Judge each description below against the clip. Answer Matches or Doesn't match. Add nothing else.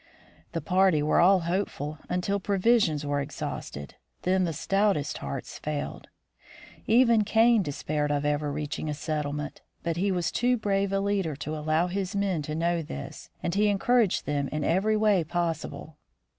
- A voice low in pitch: Doesn't match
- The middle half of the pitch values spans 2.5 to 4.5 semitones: Doesn't match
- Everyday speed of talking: Matches